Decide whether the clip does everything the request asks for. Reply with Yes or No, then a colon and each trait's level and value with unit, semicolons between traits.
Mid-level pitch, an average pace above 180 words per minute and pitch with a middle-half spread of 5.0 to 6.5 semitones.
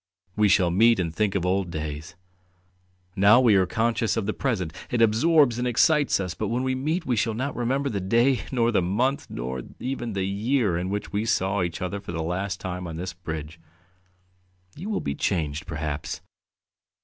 No: low, 100 Hz; average, 195 wpm; wide, 5.4 semitones